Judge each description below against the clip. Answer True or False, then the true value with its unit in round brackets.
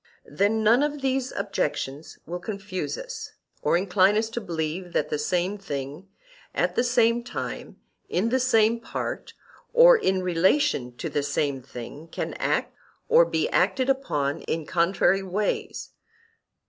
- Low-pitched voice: False (195 Hz)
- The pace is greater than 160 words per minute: False (145 wpm)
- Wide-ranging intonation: True (6.7 semitones)